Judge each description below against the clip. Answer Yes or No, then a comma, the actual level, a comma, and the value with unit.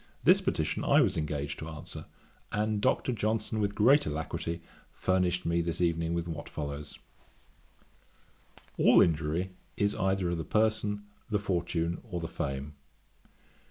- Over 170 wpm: No, average, 140 wpm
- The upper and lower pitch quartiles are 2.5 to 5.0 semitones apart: Yes, average, 4.3 semitones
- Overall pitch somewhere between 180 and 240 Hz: No, very low, 85 Hz